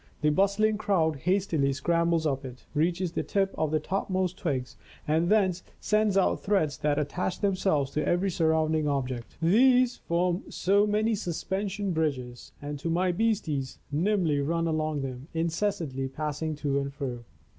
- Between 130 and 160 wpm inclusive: Yes, average, 155 wpm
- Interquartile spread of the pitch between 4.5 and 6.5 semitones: Yes, average, 4.9 semitones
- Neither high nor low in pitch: Yes, medium, 165 Hz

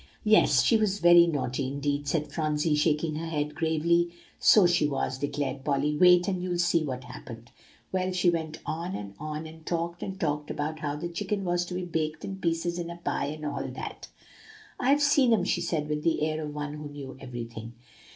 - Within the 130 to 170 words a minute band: No, fast, 205 wpm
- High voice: No, medium, 160 Hz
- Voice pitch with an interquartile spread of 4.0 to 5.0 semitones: No, average, 2.9 semitones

